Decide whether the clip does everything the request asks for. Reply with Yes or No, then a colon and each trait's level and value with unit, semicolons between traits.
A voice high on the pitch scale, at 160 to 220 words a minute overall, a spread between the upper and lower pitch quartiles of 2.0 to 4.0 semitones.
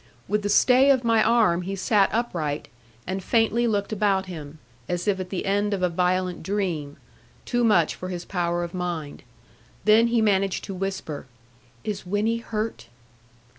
Yes: high, 195 Hz; average, 170 wpm; average, 3.4 semitones